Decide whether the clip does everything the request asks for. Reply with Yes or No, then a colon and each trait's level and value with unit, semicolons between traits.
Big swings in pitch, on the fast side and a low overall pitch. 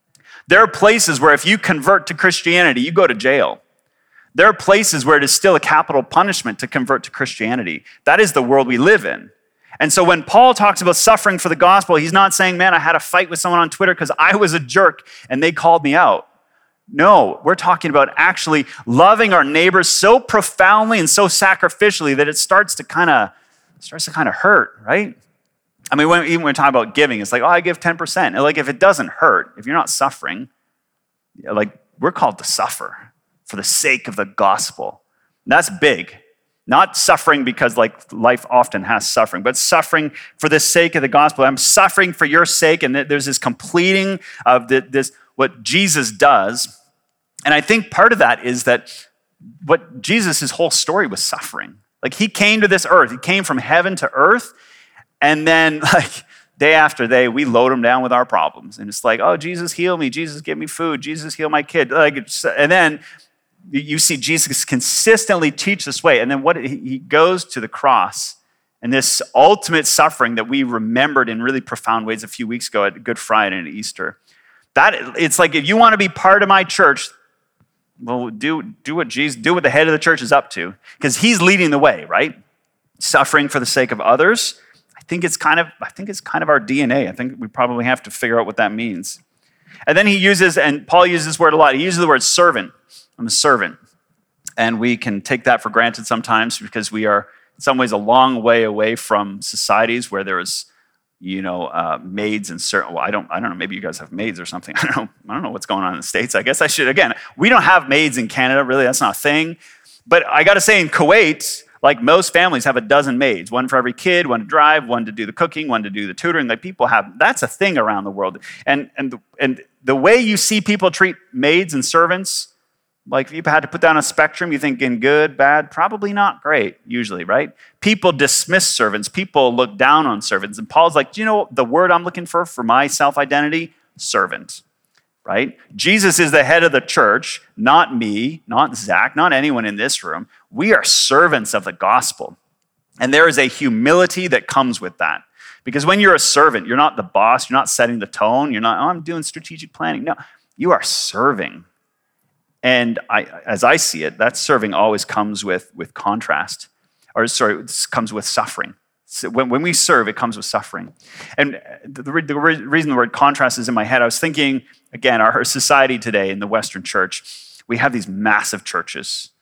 No: wide, 6.0 semitones; fast, 215 wpm; medium, 155 Hz